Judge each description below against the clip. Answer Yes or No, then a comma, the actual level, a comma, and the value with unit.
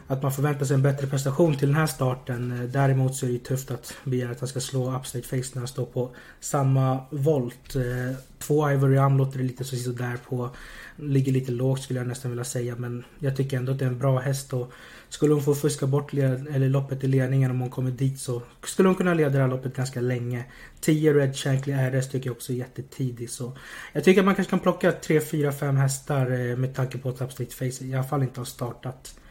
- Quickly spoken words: Yes, fast, 235 wpm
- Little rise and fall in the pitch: Yes, narrow, 1.8 semitones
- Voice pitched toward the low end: Yes, low, 130 Hz